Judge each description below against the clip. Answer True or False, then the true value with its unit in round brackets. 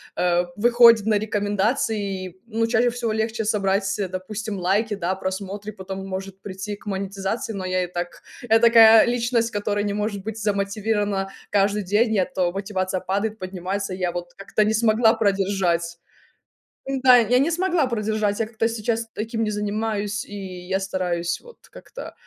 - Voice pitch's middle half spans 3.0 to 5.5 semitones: False (2.6 semitones)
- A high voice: True (205 Hz)